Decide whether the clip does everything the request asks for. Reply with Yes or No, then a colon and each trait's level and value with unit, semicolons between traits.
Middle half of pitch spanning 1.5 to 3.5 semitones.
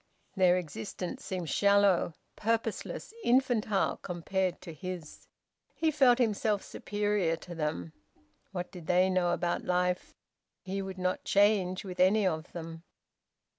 Yes: average, 2.8 semitones